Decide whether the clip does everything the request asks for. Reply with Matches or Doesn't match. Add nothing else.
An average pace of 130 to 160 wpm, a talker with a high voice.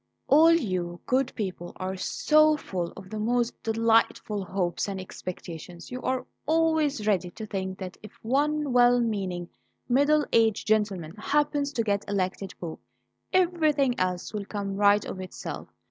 Matches